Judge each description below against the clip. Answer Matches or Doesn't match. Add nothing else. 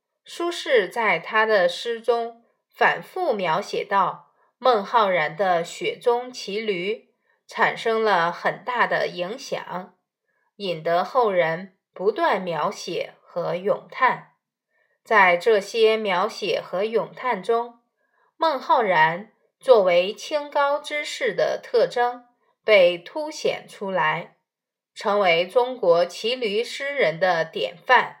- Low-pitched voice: Doesn't match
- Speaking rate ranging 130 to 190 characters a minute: Matches